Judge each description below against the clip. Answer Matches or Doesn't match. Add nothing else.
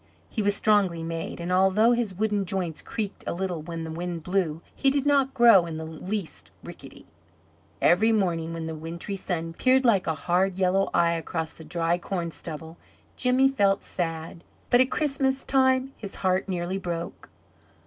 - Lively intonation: Doesn't match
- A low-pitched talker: Doesn't match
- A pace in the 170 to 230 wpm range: Matches